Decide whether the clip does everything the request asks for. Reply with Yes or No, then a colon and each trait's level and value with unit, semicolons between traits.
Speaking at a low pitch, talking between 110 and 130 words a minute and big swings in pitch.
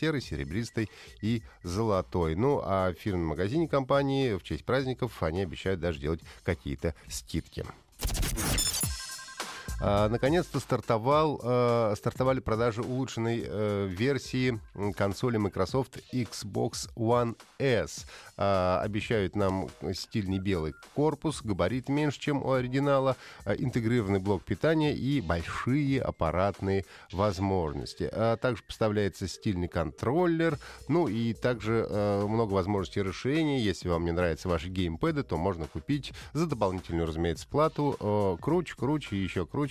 Yes: low, 105 Hz; average, 125 wpm; wide, 5.9 semitones